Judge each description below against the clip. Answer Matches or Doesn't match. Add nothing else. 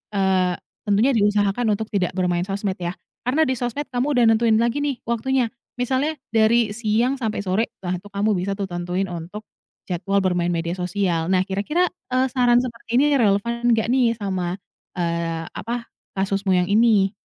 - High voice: Matches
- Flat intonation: Doesn't match